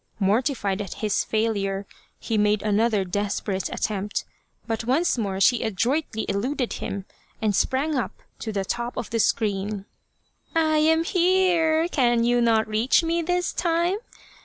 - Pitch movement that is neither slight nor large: No, wide, 7.1 semitones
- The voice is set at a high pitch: Yes, high, 230 Hz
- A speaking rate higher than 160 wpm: No, average, 150 wpm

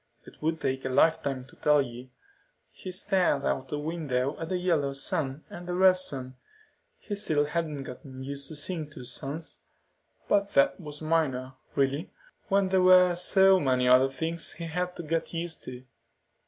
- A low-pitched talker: No, medium, 155 Hz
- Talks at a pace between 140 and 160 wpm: No, average, 175 wpm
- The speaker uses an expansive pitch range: No, average, 4.7 semitones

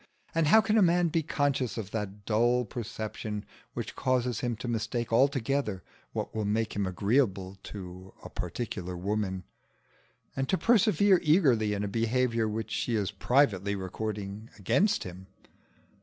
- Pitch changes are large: No, average, 4.8 semitones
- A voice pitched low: Yes, low, 110 Hz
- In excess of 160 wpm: No, average, 150 wpm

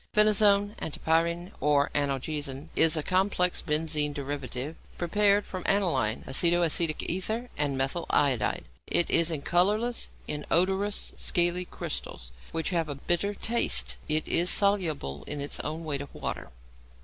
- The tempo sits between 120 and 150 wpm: Yes, slow, 135 wpm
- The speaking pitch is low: No, medium, 165 Hz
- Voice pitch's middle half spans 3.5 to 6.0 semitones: Yes, average, 4.6 semitones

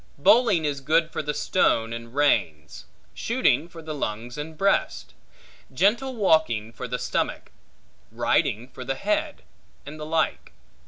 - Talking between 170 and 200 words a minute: No, average, 145 wpm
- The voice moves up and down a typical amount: No, wide, 6.1 semitones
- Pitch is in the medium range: Yes, medium, 150 Hz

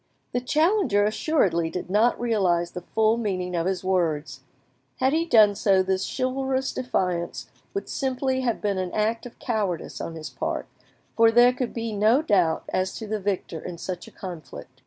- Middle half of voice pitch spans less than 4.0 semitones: No, average, 5.3 semitones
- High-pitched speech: Yes, high, 205 Hz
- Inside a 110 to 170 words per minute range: No, average, 180 wpm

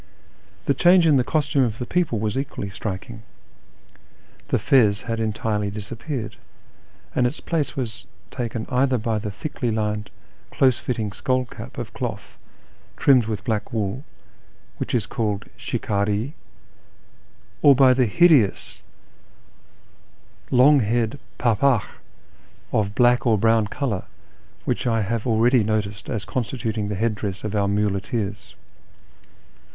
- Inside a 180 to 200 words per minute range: No, slow, 135 wpm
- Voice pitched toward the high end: No, low, 115 Hz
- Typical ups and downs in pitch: Yes, average, 3.4 semitones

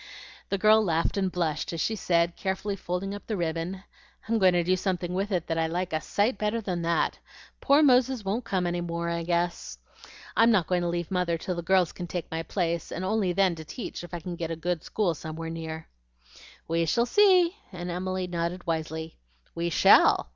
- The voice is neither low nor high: Yes, medium, 175 Hz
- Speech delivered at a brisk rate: Yes, fast, 210 wpm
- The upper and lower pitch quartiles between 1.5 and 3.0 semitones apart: Yes, average, 2.7 semitones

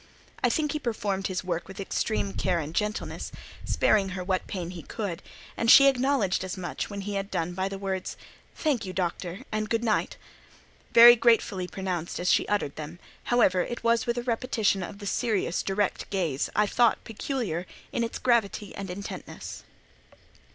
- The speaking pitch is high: Yes, high, 200 Hz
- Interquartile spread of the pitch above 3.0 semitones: Yes, average, 4.0 semitones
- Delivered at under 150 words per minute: No, average, 175 wpm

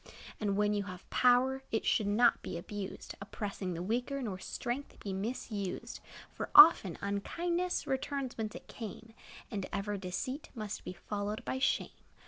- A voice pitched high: Yes, high, 210 Hz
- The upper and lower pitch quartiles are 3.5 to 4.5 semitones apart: Yes, average, 4.1 semitones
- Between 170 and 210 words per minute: No, average, 155 wpm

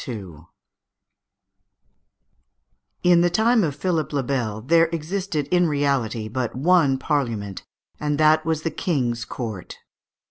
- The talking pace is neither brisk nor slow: No, slow, 120 wpm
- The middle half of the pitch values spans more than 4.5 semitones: Yes, average, 5.2 semitones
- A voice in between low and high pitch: Yes, medium, 150 Hz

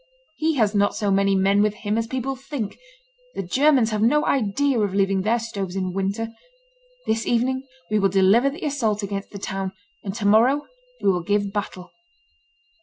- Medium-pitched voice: No, high, 210 Hz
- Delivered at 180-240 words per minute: Yes, average, 185 wpm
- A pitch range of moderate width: Yes, average, 3.9 semitones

